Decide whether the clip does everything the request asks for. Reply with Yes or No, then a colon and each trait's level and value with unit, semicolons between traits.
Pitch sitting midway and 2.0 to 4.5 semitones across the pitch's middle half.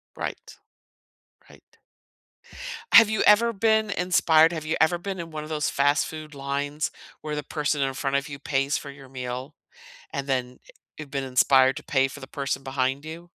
Yes: medium, 145 Hz; average, 2.8 semitones